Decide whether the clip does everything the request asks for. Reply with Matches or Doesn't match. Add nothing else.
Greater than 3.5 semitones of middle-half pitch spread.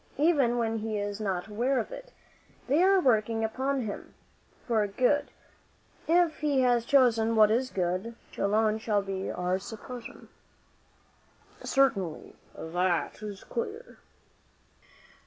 Matches